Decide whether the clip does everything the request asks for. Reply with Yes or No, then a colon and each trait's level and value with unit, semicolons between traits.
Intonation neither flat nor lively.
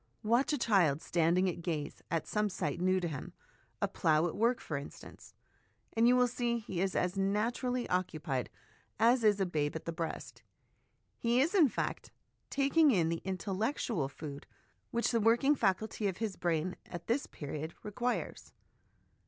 No: wide, 6.1 semitones